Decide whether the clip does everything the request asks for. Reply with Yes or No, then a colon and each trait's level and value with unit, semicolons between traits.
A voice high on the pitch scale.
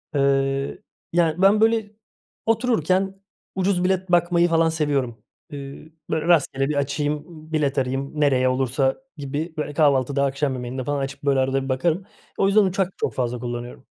No: medium, 145 Hz